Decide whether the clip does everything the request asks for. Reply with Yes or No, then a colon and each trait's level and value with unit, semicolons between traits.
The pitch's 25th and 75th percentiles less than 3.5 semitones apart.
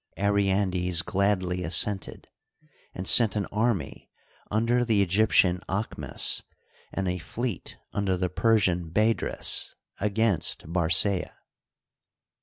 Yes: average, 2.9 semitones